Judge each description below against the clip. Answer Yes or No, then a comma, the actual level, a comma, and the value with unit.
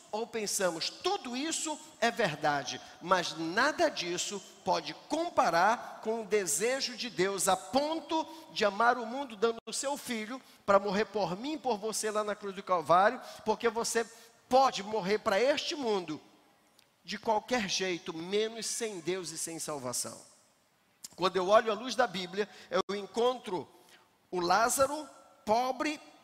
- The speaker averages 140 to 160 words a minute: Yes, average, 150 wpm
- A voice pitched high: Yes, high, 220 Hz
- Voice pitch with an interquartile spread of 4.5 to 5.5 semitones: Yes, average, 4.9 semitones